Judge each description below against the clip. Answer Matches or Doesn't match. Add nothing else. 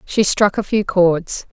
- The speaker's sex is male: Doesn't match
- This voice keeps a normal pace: Matches